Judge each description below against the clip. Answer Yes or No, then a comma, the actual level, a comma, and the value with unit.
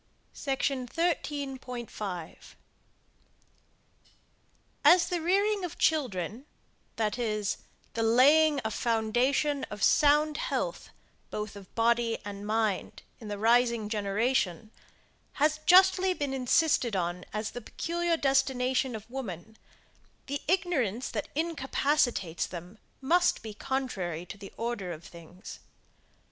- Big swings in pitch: Yes, wide, 5.8 semitones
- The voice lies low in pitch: No, high, 245 Hz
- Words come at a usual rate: No, slow, 110 wpm